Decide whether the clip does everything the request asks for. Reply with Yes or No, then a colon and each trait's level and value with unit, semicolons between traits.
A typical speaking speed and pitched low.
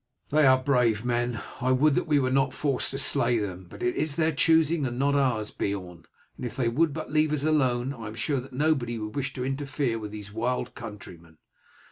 No: fast, 220 wpm; low, 130 Hz